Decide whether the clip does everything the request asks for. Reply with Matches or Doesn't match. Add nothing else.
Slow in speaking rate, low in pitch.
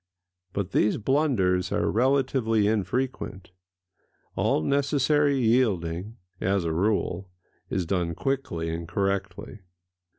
Matches